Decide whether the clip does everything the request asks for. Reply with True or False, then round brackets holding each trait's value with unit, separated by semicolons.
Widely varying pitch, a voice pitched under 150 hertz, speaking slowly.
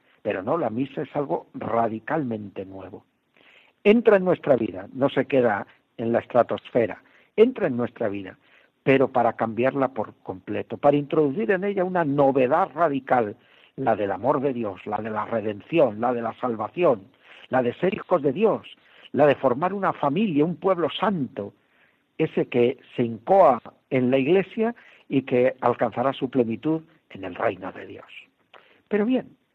False (6.2 semitones; 135 Hz; 160 wpm)